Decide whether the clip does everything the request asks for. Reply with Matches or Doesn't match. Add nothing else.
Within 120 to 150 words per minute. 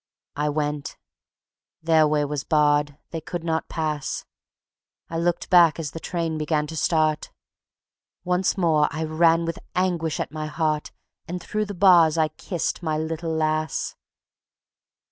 Matches